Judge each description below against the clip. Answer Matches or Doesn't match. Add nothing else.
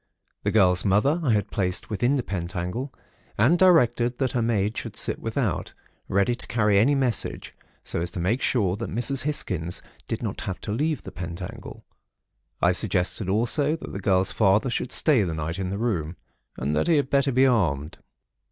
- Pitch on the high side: Doesn't match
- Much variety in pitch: Matches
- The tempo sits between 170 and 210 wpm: Matches